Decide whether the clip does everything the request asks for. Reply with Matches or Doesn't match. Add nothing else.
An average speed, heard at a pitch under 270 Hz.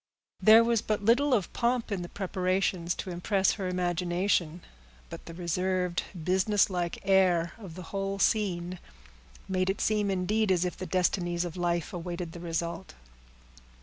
Matches